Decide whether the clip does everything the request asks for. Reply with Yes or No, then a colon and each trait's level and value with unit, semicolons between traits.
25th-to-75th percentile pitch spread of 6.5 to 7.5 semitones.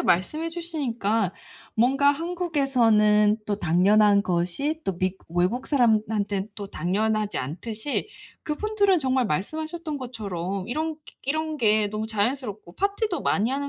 Yes: wide, 6.8 semitones